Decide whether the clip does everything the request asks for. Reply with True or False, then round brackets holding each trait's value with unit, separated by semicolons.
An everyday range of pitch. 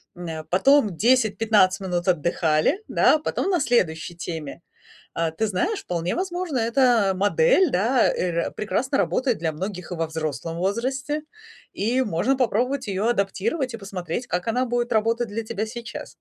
False (6.2 semitones)